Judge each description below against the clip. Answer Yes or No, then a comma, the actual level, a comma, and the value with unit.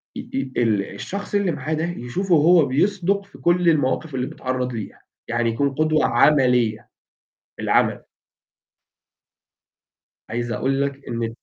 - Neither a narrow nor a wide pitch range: No, wide, 5.8 semitones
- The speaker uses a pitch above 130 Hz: Yes, medium, 140 Hz